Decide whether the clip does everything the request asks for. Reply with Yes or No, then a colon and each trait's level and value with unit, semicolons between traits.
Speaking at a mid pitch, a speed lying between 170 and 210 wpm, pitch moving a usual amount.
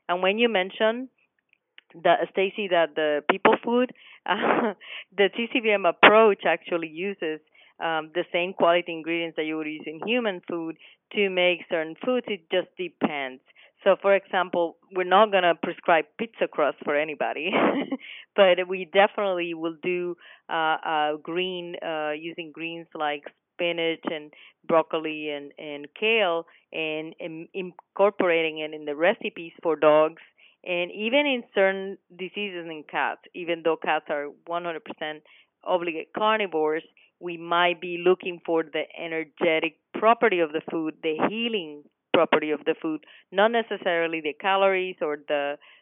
No: medium, 175 Hz; average, 145 wpm; average, 3.5 semitones